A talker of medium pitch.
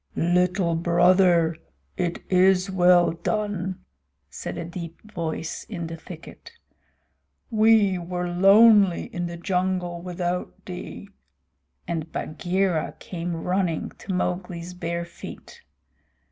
Yes: medium, 180 Hz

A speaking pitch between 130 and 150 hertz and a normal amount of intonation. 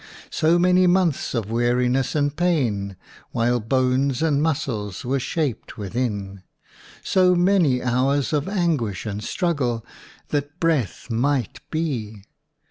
No: low, 135 Hz; wide, 5.7 semitones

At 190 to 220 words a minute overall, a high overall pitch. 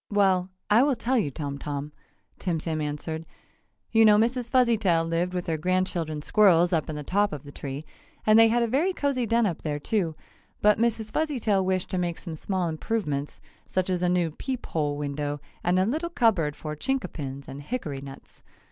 No: average, 195 wpm; medium, 180 Hz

